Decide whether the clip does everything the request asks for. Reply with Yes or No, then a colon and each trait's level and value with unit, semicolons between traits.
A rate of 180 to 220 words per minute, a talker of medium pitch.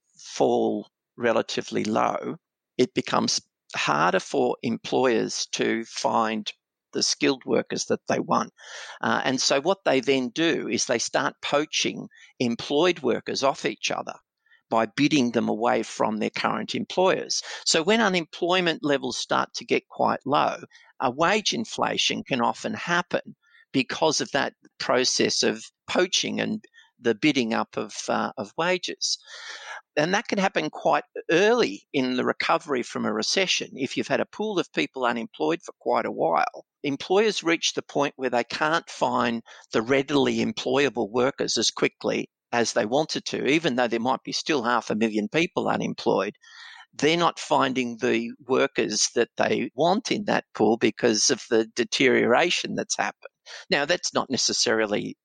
No: average, 155 wpm; medium, 145 Hz